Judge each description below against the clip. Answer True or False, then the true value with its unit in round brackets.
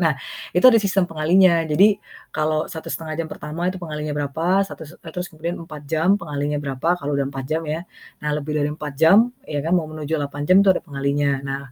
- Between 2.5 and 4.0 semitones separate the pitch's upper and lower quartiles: True (3.2 semitones)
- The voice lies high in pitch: False (155 Hz)